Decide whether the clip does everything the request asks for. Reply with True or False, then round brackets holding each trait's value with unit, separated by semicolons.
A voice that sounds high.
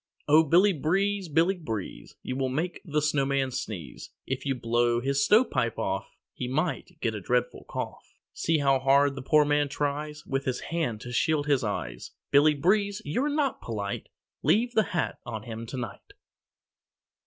False (140 Hz)